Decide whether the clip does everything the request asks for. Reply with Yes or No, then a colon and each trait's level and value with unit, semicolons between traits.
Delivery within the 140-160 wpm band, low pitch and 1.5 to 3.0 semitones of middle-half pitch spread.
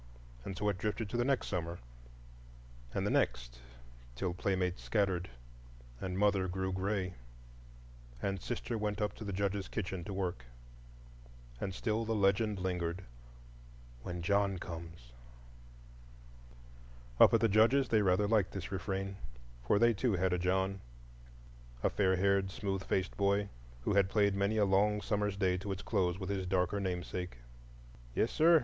Yes: average, 150 wpm; very low, 95 Hz; narrow, 2.6 semitones